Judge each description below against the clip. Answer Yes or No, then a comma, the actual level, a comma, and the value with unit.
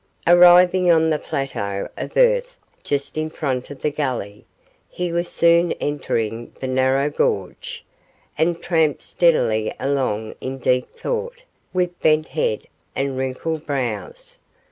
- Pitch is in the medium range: Yes, medium, 155 Hz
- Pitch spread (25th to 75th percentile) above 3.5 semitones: Yes, average, 5.1 semitones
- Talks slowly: Yes, slow, 130 wpm